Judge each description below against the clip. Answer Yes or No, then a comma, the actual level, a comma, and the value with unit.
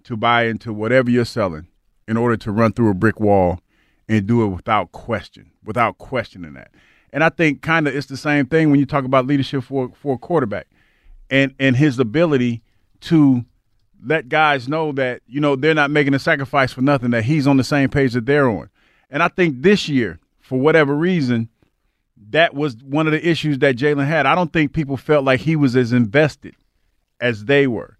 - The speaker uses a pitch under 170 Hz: Yes, low, 135 Hz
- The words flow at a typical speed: No, fast, 210 wpm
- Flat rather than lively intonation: No, average, 4.0 semitones